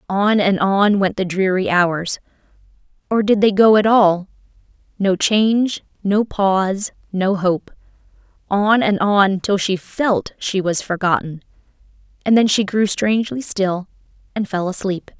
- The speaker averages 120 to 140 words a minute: Yes, slow, 135 wpm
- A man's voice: No, female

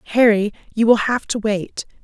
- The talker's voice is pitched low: No, high, 215 Hz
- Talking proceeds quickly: No, average, 175 wpm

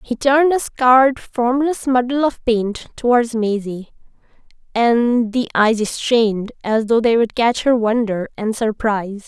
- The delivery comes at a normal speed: Yes, average, 150 wpm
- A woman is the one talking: Yes, female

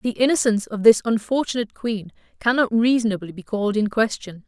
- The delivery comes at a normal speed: Yes, average, 160 wpm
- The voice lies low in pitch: No, high, 220 Hz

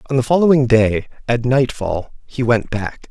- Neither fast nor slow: Yes, average, 175 wpm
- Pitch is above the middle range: No, low, 120 Hz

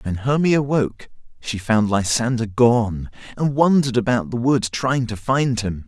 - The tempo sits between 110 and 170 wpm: Yes, average, 165 wpm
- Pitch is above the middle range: No, low, 120 Hz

